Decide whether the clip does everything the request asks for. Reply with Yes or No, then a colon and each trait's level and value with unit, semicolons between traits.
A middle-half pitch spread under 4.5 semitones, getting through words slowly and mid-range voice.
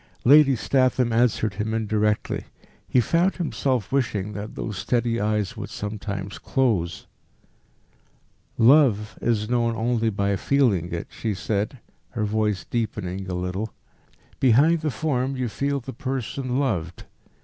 No: average, 4.1 semitones; slow, 130 wpm; low, 115 Hz